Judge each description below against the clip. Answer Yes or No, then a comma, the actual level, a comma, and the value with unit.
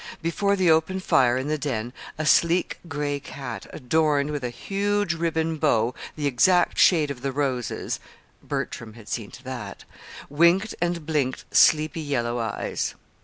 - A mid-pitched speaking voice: Yes, medium, 145 Hz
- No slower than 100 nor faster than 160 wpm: Yes, average, 155 wpm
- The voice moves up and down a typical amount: Yes, average, 4.7 semitones